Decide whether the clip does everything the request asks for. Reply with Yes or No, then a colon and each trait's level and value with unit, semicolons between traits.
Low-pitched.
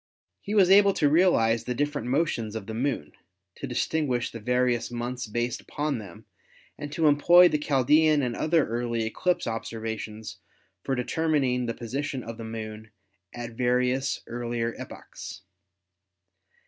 Yes: low, 125 Hz